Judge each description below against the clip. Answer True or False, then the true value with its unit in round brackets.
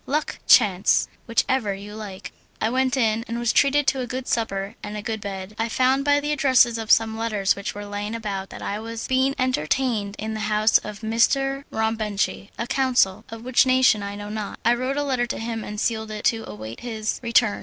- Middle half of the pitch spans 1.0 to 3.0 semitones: False (3.6 semitones)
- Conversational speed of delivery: False (215 wpm)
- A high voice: True (225 Hz)